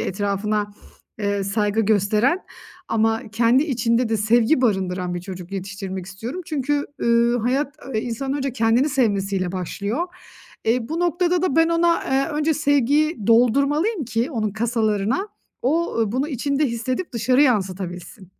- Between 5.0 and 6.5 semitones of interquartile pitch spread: Yes, wide, 5.5 semitones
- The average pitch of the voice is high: Yes, high, 235 Hz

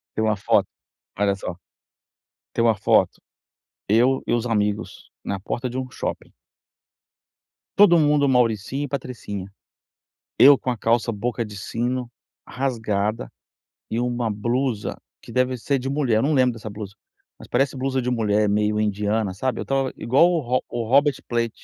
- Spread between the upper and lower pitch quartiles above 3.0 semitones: Yes, average, 3.5 semitones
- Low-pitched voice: Yes, low, 120 Hz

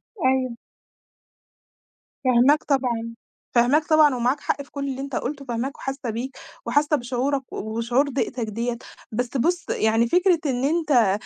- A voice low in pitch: No, very high, 260 Hz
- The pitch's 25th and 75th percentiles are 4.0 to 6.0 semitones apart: No, average, 3.2 semitones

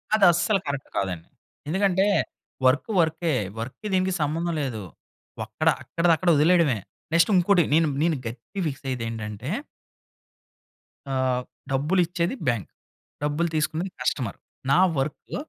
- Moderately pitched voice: Yes, medium, 155 Hz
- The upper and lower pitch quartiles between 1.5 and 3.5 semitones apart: No, average, 5.2 semitones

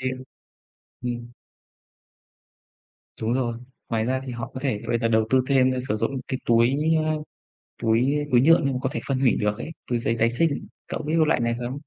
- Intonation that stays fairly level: Yes, narrow, 2.3 semitones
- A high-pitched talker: No, low, 125 Hz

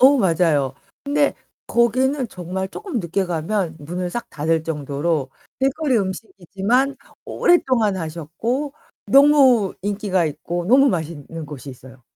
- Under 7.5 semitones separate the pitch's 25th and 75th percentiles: No, wide, 7.9 semitones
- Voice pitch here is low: No, high, 190 Hz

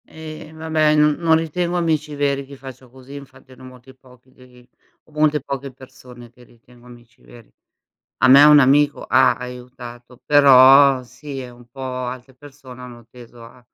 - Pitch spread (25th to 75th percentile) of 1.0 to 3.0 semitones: Yes, average, 2.7 semitones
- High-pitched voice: No, low, 130 Hz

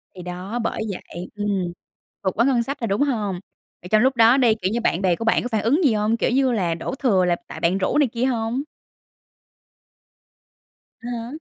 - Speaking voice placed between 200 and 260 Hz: Yes, high, 225 Hz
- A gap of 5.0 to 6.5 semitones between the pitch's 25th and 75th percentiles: No, average, 4.4 semitones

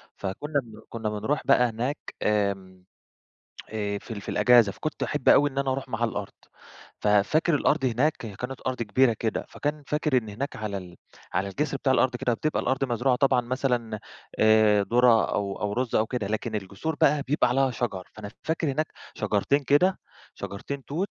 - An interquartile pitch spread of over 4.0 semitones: Yes, average, 4.6 semitones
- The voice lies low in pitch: Yes, low, 120 Hz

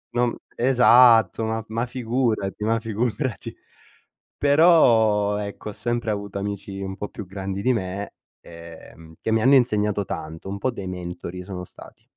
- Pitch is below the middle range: Yes, low, 105 Hz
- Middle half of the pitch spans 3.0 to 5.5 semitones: Yes, average, 3.4 semitones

